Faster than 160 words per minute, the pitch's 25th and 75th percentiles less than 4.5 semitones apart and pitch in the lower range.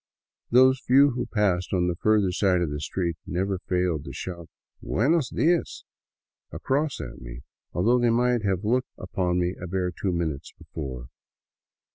No: average, 175 wpm; wide, 5.6 semitones; very low, 95 Hz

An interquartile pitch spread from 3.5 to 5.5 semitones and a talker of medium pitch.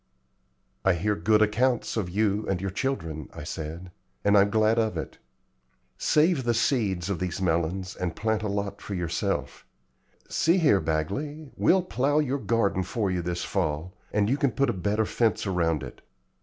No: average, 4.7 semitones; low, 100 Hz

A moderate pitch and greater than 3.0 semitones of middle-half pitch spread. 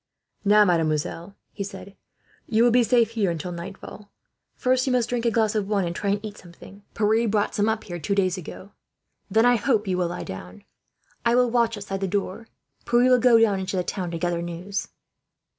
No: high, 205 Hz; average, 4.0 semitones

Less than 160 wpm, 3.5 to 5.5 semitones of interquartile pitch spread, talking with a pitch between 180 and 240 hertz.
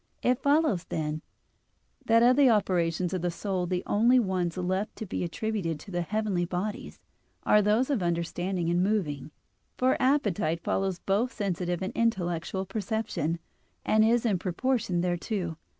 Yes: average, 150 wpm; average, 3.9 semitones; high, 190 Hz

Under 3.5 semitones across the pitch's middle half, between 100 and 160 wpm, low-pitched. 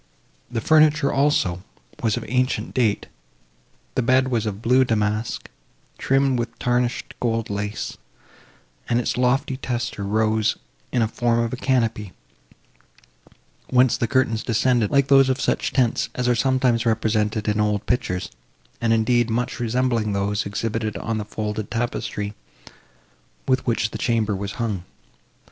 Yes: average, 2.9 semitones; average, 145 wpm; low, 115 Hz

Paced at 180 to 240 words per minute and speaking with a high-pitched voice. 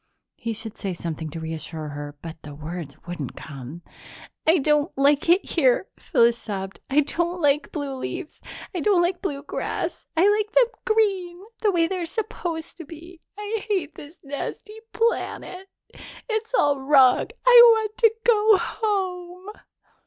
No: average, 155 wpm; very high, 330 Hz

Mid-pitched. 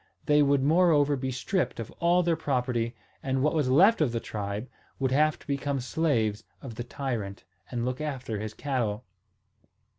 No: low, 130 Hz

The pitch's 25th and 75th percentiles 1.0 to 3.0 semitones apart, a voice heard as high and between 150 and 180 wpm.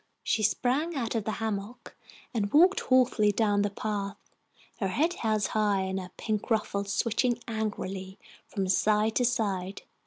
Yes: average, 2.7 semitones; high, 215 Hz; average, 155 wpm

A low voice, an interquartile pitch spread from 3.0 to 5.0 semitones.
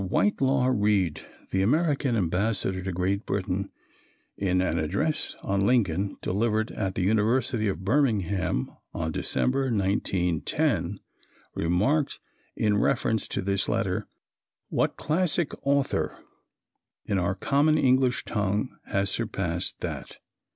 No: low, 100 Hz; wide, 5.4 semitones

